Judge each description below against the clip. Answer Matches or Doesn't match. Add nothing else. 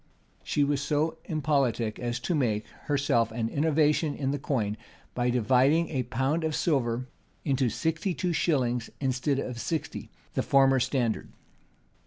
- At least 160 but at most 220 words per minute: Doesn't match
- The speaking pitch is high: Doesn't match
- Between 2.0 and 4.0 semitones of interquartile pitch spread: Matches